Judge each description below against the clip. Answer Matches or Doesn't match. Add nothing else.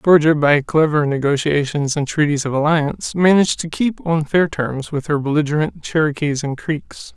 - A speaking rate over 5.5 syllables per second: Doesn't match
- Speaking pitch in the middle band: Matches